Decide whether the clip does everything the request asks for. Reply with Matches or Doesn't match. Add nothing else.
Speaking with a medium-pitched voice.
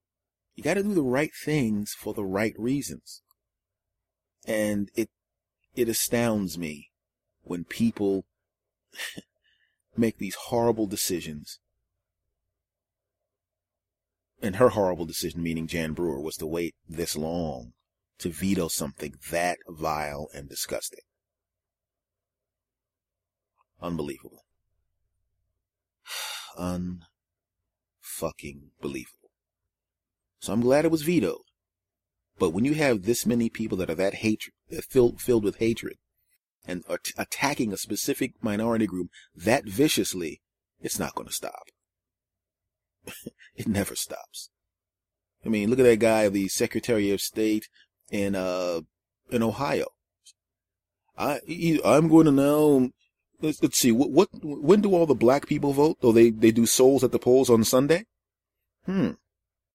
Doesn't match